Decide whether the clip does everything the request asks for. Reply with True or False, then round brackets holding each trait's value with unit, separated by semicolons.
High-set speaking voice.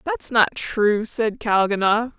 True (220 Hz)